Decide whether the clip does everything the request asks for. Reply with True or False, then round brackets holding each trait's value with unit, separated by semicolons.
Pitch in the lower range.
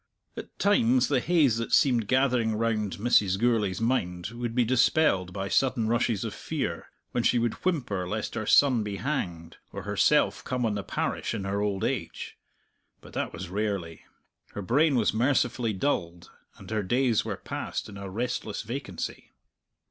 True (115 Hz)